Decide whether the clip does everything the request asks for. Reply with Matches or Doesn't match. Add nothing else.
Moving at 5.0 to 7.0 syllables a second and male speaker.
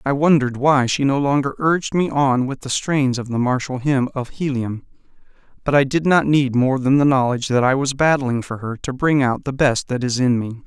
Matches